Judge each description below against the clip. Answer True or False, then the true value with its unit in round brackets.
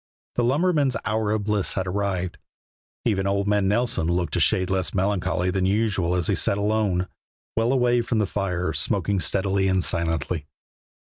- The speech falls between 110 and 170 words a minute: True (165 wpm)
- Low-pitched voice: True (100 Hz)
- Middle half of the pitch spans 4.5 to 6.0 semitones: False (3.0 semitones)